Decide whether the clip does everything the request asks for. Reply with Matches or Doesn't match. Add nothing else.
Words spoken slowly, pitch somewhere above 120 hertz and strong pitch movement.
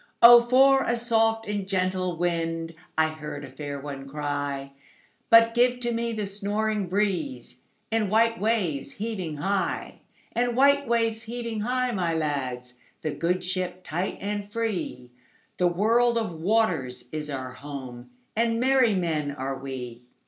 Matches